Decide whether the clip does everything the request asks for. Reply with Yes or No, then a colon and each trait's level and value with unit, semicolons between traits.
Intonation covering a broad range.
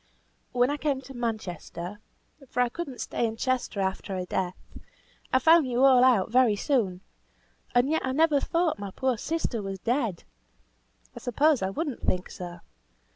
Yes: wide, 5.8 semitones